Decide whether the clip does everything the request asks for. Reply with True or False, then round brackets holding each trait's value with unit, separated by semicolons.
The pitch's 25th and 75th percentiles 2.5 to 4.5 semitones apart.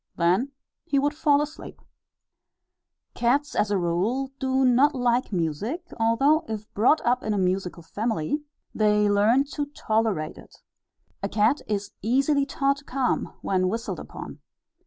False (5.3 semitones)